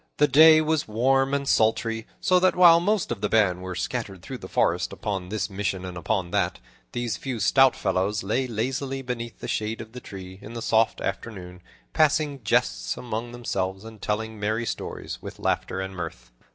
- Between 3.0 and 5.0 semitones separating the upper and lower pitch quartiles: No, wide, 5.6 semitones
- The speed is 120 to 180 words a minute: No, average, 190 wpm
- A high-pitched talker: No, low, 110 Hz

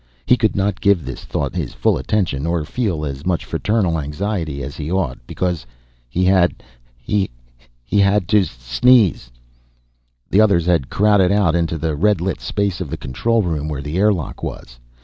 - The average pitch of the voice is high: No, very low, 90 Hz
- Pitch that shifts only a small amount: No, average, 5.2 semitones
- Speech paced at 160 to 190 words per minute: Yes, average, 170 wpm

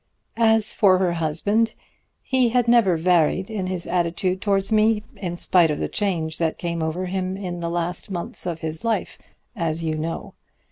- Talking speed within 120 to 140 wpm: No, average, 180 wpm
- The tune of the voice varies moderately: Yes, average, 3.4 semitones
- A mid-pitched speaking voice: Yes, medium, 180 Hz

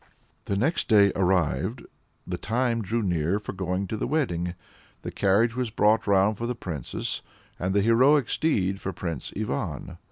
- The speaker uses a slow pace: No, average, 165 wpm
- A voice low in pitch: Yes, low, 100 Hz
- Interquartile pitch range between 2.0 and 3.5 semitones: No, average, 4.0 semitones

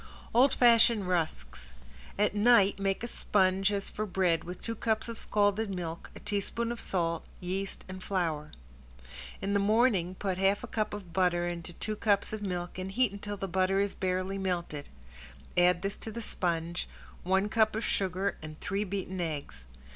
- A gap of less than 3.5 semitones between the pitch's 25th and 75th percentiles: Yes, average, 2.7 semitones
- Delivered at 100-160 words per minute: No, average, 175 wpm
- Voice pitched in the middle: No, high, 195 Hz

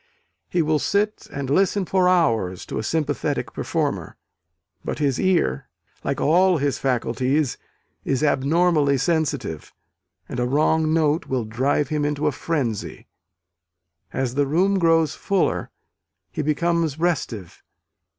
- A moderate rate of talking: No, slow, 130 wpm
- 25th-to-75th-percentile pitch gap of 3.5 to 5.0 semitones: Yes, average, 4.1 semitones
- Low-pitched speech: No, medium, 150 Hz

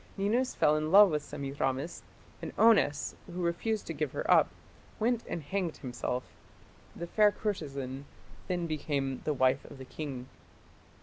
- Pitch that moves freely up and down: Yes, wide, 6.0 semitones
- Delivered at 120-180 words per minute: Yes, average, 150 wpm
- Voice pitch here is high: No, medium, 155 Hz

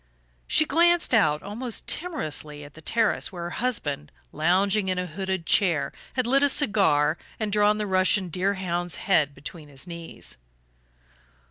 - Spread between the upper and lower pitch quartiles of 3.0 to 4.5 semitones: No, average, 5.2 semitones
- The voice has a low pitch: No, medium, 185 Hz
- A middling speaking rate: Yes, average, 150 wpm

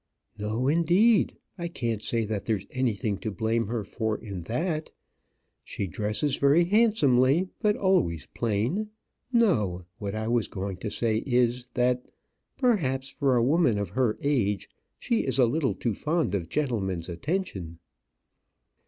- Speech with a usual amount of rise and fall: No, wide, 6.6 semitones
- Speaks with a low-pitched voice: Yes, low, 120 Hz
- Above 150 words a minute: No, average, 145 wpm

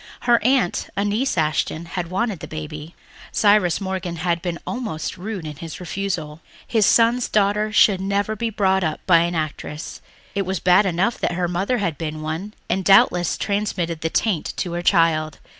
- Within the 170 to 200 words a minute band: Yes, average, 180 wpm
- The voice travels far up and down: No, average, 3.7 semitones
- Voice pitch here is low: No, medium, 180 Hz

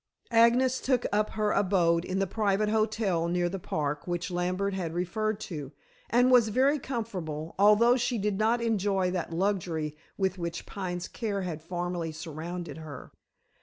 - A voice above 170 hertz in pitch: Yes, high, 190 Hz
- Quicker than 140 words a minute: Yes, average, 160 wpm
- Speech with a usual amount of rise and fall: Yes, average, 4.1 semitones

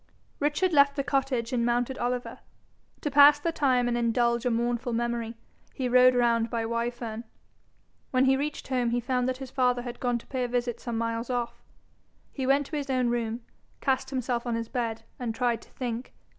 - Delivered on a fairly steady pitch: Yes, narrow, 1.9 semitones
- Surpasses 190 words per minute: Yes, average, 200 wpm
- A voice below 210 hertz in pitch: No, high, 245 Hz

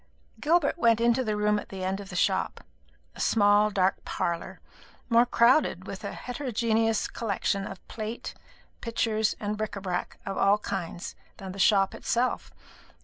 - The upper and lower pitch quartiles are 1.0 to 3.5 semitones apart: Yes, average, 3.0 semitones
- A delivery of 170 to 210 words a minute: No, average, 160 wpm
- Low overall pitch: No, high, 210 Hz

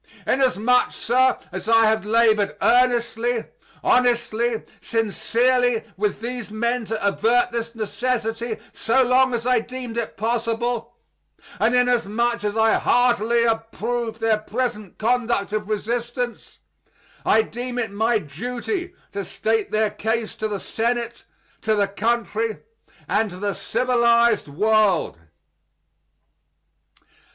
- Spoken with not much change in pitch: Yes, narrow, 2.0 semitones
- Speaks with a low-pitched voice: No, high, 230 Hz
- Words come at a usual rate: No, slow, 120 wpm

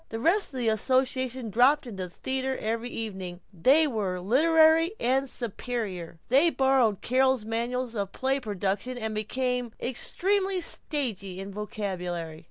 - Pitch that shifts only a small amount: No, average, 4.4 semitones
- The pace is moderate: Yes, average, 150 wpm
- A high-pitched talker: Yes, high, 240 Hz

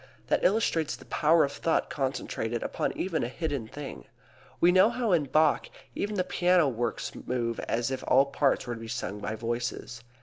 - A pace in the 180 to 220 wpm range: Yes, average, 190 wpm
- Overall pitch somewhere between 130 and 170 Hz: Yes, medium, 140 Hz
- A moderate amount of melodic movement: No, wide, 6.1 semitones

